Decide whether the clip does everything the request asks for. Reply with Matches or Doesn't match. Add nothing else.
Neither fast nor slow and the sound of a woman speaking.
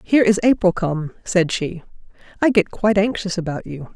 Matches